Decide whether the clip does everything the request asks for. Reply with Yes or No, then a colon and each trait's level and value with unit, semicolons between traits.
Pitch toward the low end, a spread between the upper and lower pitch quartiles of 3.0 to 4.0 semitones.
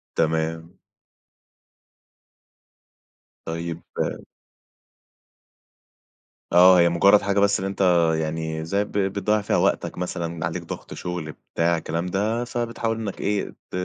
Yes: very low, 90 Hz; average, 3.6 semitones